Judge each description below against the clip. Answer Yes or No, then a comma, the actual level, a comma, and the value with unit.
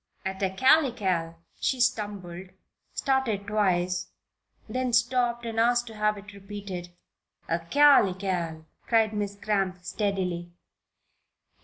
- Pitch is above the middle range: Yes, high, 205 Hz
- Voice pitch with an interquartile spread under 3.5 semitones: No, average, 4.4 semitones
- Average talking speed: No, slow, 100 wpm